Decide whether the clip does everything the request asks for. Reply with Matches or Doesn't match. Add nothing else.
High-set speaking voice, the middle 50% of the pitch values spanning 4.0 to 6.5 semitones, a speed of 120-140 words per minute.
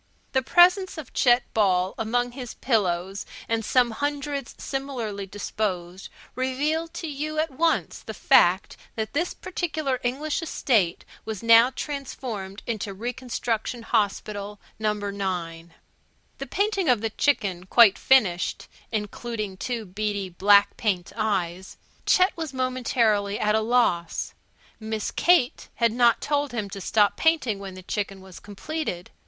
Matches